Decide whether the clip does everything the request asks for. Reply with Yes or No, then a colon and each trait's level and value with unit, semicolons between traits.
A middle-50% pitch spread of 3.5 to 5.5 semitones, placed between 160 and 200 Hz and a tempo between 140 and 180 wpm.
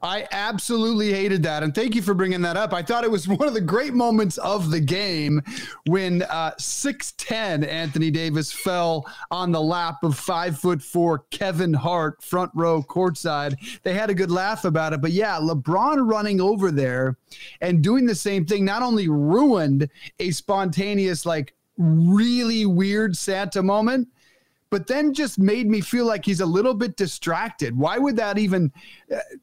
Yes: average, 4.8 semitones; medium, 185 Hz; average, 170 wpm